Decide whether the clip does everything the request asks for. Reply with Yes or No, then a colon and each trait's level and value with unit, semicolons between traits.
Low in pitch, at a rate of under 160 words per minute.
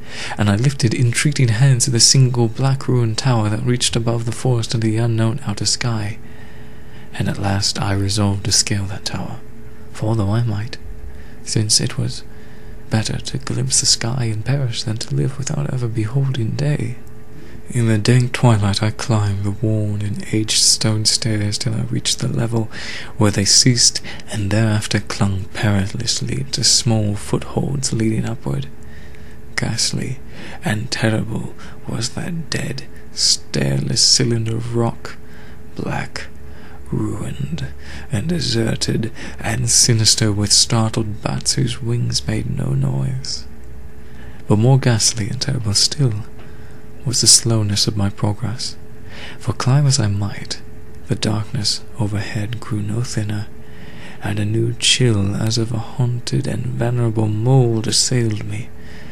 Yes: low, 110 Hz; average, 140 wpm